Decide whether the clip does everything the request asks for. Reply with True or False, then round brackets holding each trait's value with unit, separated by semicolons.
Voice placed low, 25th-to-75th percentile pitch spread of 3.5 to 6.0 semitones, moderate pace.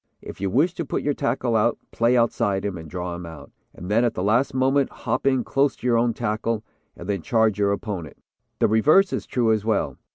False (110 Hz; 4.1 semitones; 230 wpm)